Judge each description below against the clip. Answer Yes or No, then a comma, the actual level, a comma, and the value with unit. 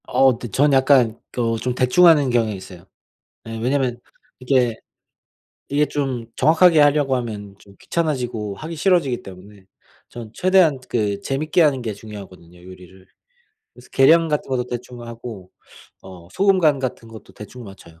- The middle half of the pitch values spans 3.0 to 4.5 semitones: No, wide, 5.4 semitones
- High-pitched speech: No, low, 125 Hz